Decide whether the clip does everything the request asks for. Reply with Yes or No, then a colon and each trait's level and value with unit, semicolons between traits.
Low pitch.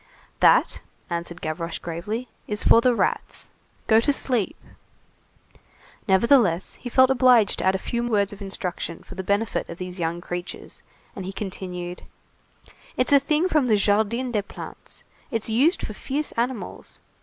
No: high, 210 Hz